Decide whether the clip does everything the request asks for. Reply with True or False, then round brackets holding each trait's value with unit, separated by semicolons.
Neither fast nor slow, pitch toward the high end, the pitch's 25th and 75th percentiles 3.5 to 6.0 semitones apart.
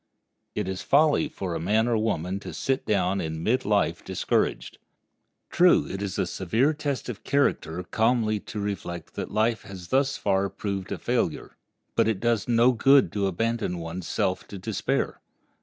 False (175 wpm; 105 Hz; 4.1 semitones)